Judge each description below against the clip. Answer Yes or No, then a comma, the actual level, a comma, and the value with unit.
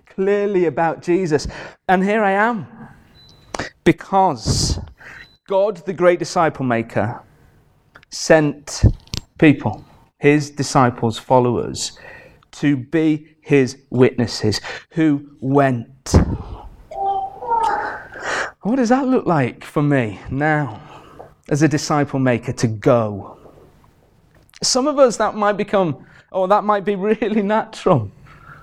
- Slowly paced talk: Yes, slow, 105 wpm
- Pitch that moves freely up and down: Yes, wide, 7.0 semitones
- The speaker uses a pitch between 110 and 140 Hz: No, medium, 155 Hz